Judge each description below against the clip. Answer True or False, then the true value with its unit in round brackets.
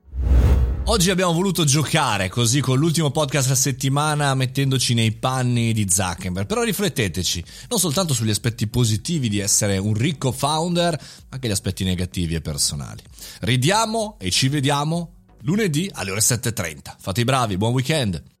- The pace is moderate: True (155 wpm)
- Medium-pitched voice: False (130 Hz)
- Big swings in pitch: True (7.1 semitones)